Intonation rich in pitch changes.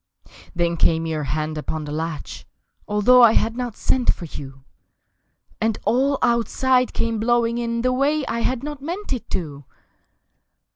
Yes: wide, 7.7 semitones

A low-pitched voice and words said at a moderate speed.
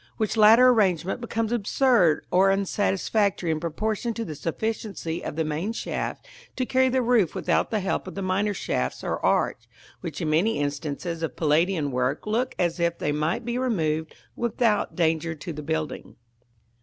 No: medium, 185 Hz; average, 170 wpm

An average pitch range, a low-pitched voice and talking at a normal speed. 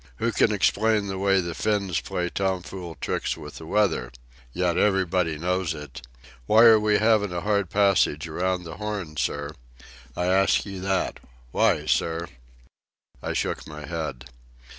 Yes: average, 3.5 semitones; very low, 90 Hz; average, 160 wpm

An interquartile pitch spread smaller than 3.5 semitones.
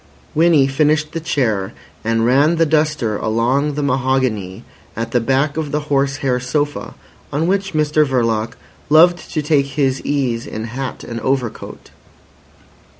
No: average, 4.0 semitones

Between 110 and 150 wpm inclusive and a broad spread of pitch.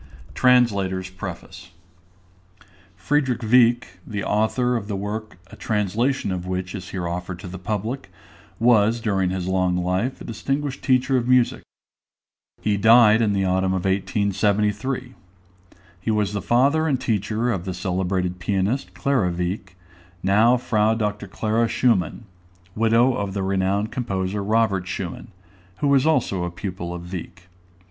No: average, 145 wpm; average, 4.0 semitones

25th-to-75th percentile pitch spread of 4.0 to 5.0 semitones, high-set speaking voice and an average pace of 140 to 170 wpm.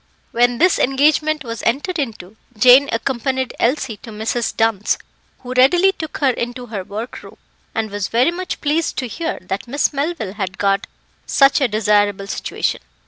Yes: average, 4.7 semitones; high, 245 Hz; average, 165 wpm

